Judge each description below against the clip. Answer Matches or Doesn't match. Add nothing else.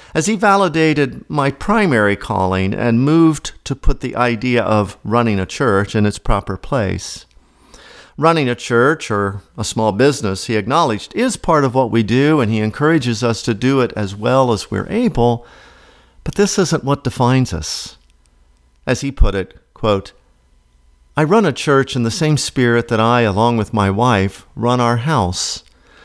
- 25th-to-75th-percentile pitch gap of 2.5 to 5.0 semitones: Doesn't match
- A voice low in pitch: Matches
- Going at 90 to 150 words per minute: Doesn't match